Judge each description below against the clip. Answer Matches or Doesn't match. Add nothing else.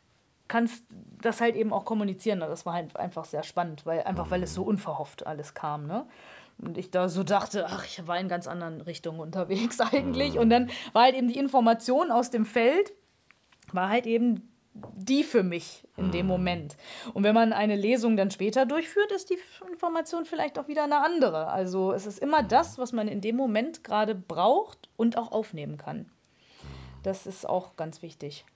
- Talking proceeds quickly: Matches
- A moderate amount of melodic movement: Doesn't match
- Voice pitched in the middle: Doesn't match